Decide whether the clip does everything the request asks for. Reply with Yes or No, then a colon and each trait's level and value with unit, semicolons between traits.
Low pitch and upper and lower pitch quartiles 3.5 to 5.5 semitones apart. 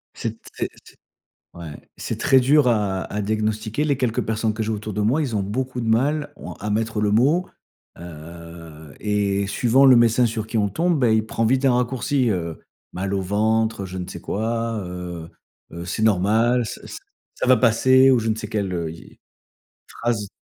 Yes: low, 110 Hz; average, 3.8 semitones